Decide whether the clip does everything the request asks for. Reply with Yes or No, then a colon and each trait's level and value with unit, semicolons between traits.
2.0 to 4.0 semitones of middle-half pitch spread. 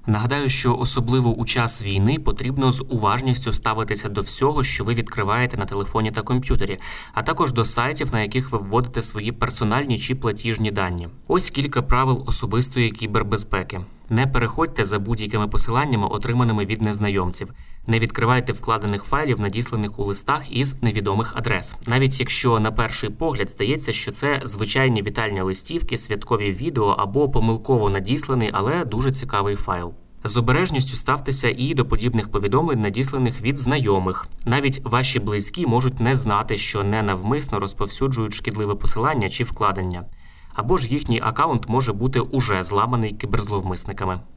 Yes: average, 3.5 semitones